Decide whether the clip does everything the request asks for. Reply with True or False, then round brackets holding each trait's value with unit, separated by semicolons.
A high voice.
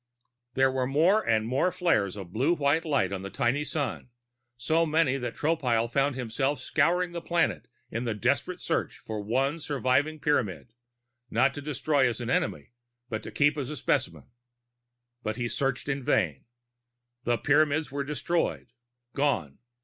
False (135 Hz)